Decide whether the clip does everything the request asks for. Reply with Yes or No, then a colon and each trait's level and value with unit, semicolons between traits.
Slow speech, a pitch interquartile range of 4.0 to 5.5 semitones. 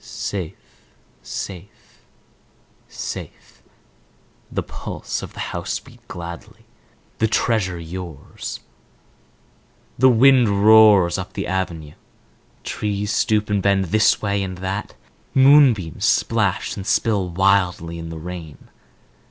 No: slow, 105 wpm; average, 3.4 semitones